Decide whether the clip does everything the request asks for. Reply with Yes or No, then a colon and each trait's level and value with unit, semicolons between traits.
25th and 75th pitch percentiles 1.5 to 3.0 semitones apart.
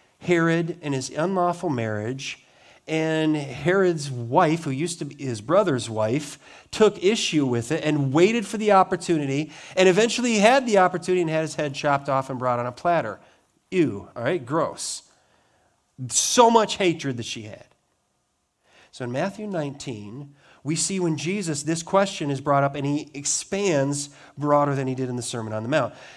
No: average, 4.8 semitones